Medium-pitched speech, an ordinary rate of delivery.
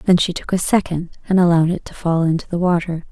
No: medium, 175 Hz; fast, 250 wpm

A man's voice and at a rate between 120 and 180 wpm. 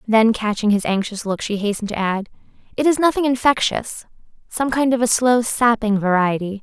No: female; average, 170 wpm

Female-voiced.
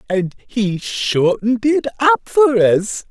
No: male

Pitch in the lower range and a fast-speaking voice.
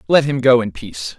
Yes: low, 125 Hz; fast, 255 wpm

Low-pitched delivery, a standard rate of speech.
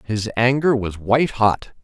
Yes: low, 115 Hz; average, 165 wpm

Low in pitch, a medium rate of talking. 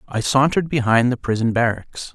Yes: low, 125 Hz; average, 170 wpm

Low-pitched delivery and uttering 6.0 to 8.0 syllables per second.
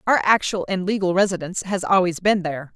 No: medium, 185 Hz; 6.3 syllables/s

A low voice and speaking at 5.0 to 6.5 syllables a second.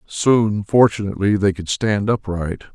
No: low, 100 Hz; 4.4 syllables/s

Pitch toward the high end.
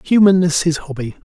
No: medium, 165 Hz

